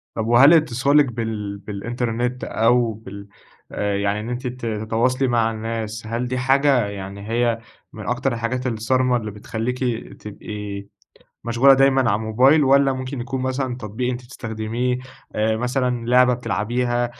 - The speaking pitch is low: Yes, low, 120 Hz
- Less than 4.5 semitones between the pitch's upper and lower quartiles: Yes, narrow, 2.5 semitones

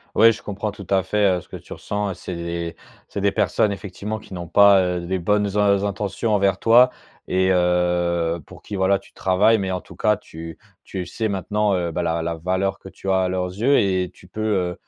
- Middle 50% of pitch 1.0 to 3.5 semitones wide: Yes, narrow, 2.6 semitones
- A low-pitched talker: Yes, very low, 95 Hz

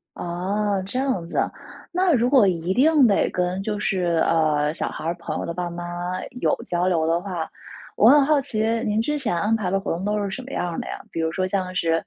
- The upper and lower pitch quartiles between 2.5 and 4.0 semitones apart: No, average, 4.4 semitones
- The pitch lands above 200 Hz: No, high, 190 Hz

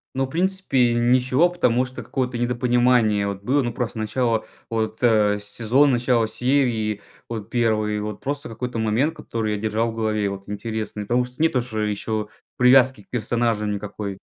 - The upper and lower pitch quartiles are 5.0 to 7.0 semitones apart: No, average, 2.8 semitones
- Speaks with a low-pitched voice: Yes, low, 115 Hz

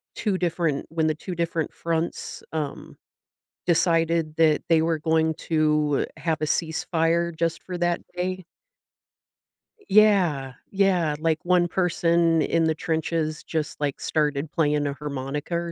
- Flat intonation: Yes, narrow, 1.8 semitones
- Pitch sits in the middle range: Yes, medium, 165 Hz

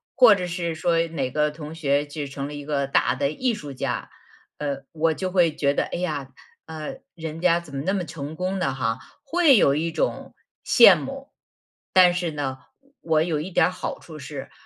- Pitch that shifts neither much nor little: Yes, average, 3.8 semitones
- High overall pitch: No, medium, 155 Hz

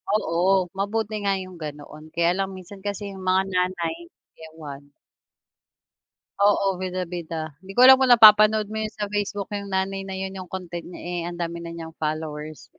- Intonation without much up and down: No, average, 3.2 semitones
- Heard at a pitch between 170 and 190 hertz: Yes, medium, 185 Hz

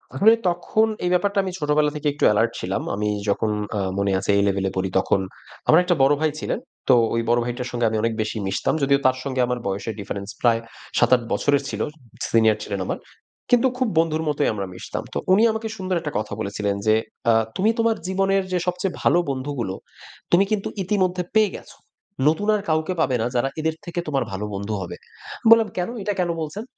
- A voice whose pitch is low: No, medium, 145 Hz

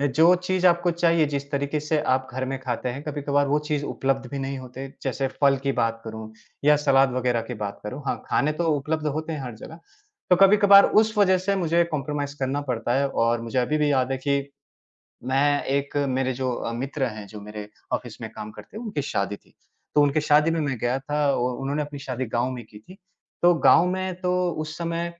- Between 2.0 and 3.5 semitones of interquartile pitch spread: Yes, average, 3.2 semitones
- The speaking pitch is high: No, medium, 140 Hz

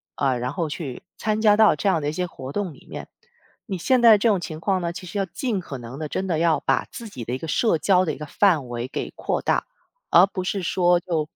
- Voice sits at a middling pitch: Yes, medium, 175 Hz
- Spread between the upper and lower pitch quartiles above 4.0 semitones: Yes, average, 4.8 semitones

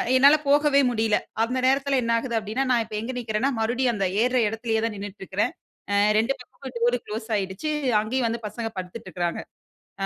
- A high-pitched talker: Yes, high, 230 Hz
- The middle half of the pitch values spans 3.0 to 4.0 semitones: Yes, average, 3.3 semitones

